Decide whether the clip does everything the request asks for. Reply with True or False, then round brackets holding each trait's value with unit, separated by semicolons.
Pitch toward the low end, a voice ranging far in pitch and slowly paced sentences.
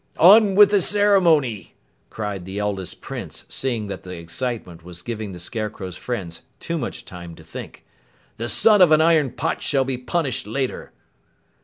False (120 Hz; 8.9 semitones; 165 wpm)